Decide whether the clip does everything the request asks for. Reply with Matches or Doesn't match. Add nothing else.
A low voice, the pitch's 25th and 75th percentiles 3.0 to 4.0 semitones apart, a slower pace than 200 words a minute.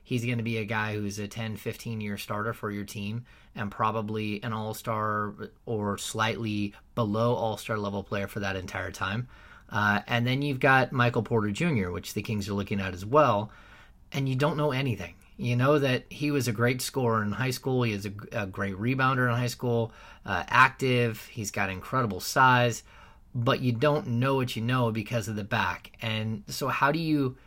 Doesn't match